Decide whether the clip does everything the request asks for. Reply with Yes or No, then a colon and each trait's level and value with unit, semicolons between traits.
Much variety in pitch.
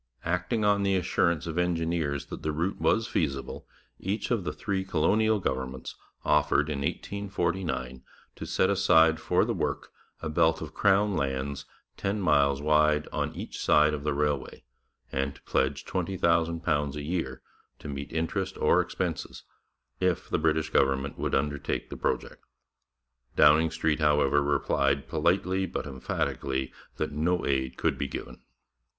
No: average, 4.2 semitones